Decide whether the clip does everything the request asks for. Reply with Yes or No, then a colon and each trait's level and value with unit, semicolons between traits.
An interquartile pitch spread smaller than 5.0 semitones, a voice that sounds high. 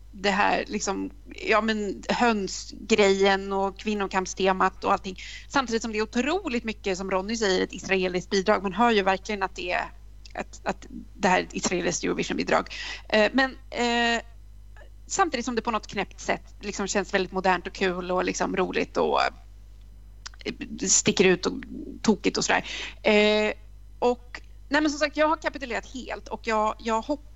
Yes: average, 3.7 semitones; high, 215 Hz